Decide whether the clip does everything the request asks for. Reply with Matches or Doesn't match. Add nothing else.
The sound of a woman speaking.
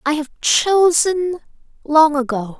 Matches